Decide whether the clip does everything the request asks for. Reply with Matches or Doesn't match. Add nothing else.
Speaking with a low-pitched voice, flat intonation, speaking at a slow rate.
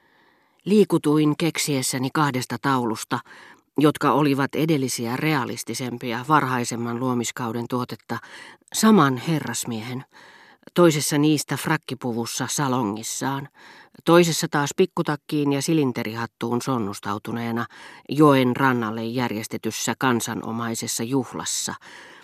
Doesn't match